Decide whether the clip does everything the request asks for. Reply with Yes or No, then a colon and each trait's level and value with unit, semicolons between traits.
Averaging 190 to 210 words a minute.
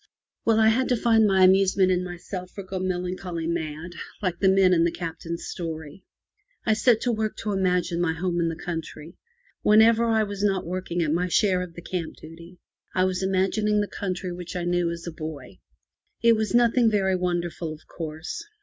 Yes: average, 195 wpm